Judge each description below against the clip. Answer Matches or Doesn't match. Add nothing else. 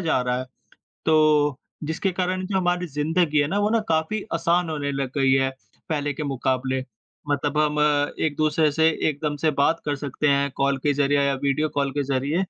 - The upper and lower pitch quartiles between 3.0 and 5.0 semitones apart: Doesn't match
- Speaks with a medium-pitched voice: Matches